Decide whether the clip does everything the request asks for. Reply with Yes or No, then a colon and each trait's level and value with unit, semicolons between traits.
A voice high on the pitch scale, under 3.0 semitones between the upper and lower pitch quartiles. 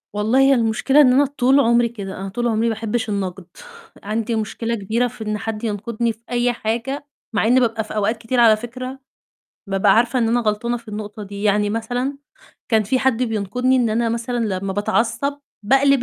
Yes: high, 230 Hz; narrow, 2.5 semitones